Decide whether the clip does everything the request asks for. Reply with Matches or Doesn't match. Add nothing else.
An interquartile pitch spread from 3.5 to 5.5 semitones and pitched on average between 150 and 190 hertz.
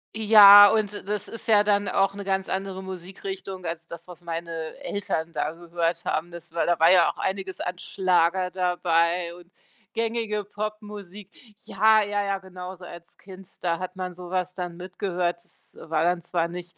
Doesn't match